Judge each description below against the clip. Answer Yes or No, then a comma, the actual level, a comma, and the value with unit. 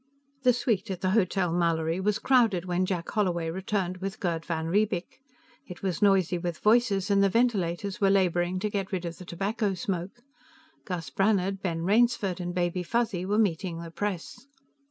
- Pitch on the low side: No, high, 190 Hz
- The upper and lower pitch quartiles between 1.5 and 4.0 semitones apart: Yes, average, 2.8 semitones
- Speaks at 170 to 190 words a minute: Yes, average, 175 wpm